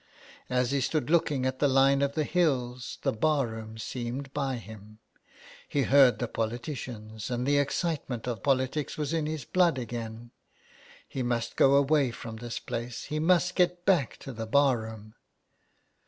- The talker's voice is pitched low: Yes, low, 130 Hz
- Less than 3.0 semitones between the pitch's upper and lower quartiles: No, average, 3.6 semitones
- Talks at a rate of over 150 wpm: Yes, average, 175 wpm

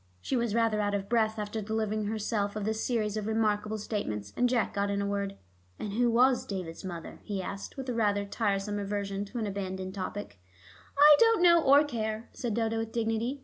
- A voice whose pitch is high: Yes, high, 215 Hz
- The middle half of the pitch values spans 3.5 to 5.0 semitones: No, narrow, 2.4 semitones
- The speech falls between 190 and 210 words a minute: Yes, fast, 205 wpm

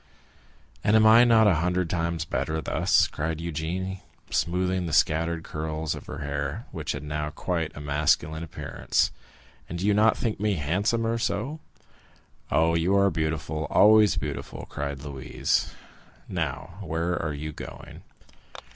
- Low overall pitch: Yes, very low, 85 Hz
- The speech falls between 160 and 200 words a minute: No, average, 145 wpm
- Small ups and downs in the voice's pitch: No, average, 4.1 semitones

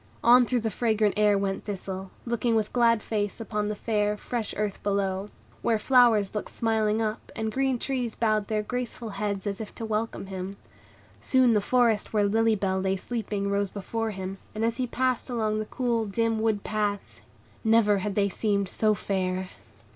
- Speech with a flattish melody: Yes, narrow, 2.2 semitones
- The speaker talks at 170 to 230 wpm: Yes, average, 185 wpm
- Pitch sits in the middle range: No, high, 215 Hz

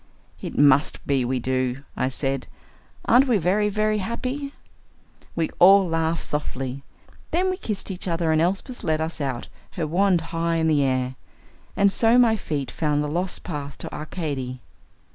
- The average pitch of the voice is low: No, medium, 165 Hz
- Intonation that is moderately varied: No, wide, 6.0 semitones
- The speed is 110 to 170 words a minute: Yes, average, 165 wpm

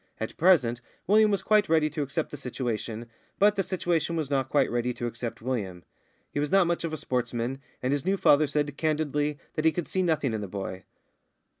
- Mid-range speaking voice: Yes, medium, 145 Hz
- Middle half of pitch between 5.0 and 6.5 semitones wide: Yes, wide, 5.5 semitones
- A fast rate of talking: Yes, fast, 210 wpm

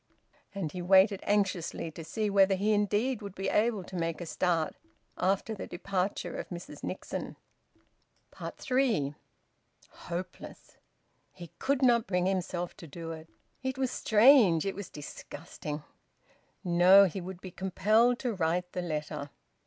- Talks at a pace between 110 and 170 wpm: Yes, average, 145 wpm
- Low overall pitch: No, medium, 185 Hz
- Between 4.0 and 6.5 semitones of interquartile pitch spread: No, average, 3.3 semitones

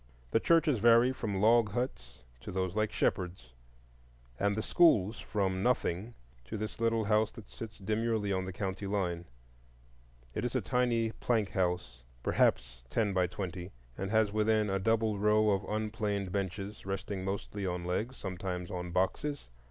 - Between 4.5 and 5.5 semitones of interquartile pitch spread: No, average, 3.0 semitones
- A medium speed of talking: Yes, average, 160 wpm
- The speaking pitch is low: Yes, low, 100 Hz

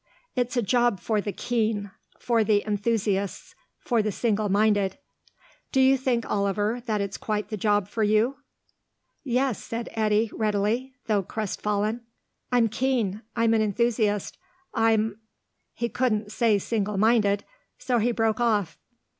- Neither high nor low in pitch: No, high, 220 Hz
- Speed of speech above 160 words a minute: No, average, 145 wpm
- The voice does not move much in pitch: Yes, narrow, 2.3 semitones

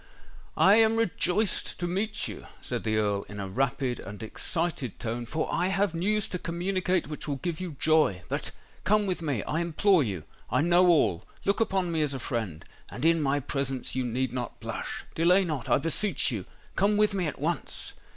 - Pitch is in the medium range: Yes, medium, 160 Hz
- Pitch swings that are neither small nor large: No, wide, 6.6 semitones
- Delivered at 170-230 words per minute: Yes, average, 175 wpm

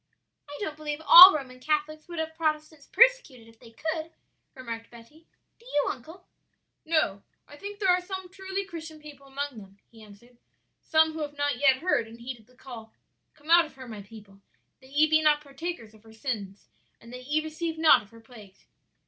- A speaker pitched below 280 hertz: No, very high, 290 Hz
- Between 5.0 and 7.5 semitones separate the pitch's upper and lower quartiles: Yes, wide, 5.4 semitones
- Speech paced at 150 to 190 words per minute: No, average, 200 wpm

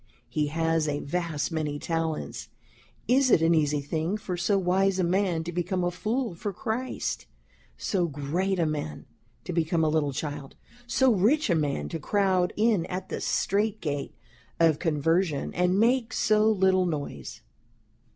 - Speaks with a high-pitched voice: No, medium, 175 Hz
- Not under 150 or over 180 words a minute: Yes, average, 160 wpm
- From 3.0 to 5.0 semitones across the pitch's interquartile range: Yes, average, 4.0 semitones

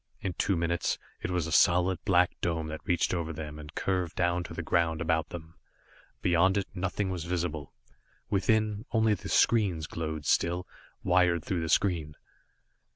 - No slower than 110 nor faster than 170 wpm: Yes, average, 165 wpm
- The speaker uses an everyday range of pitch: No, narrow, 2.3 semitones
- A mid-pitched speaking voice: No, very low, 85 Hz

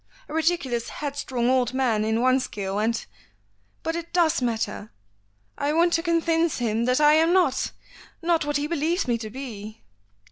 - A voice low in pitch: No, very high, 265 Hz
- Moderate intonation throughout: No, wide, 6.2 semitones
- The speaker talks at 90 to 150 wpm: No, average, 175 wpm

